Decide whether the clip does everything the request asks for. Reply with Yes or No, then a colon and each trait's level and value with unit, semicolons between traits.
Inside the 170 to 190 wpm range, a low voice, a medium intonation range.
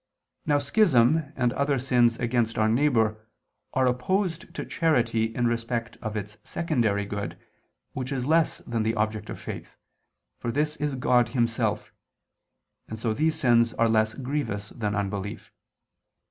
No: average, 145 wpm; low, 120 Hz; average, 4.1 semitones